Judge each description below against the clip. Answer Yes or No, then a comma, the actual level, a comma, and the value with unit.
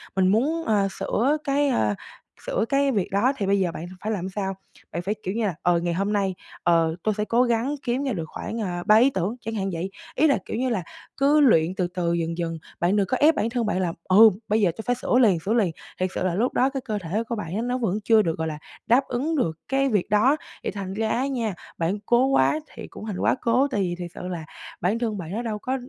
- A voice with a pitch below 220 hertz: Yes, high, 210 Hz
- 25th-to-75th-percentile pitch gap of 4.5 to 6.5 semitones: Yes, average, 5.2 semitones